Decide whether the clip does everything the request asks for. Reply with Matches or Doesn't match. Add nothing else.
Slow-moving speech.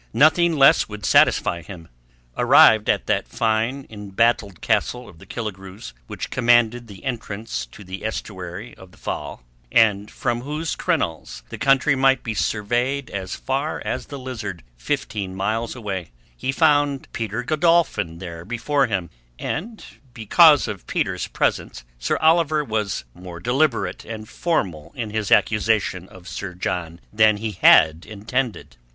Doesn't match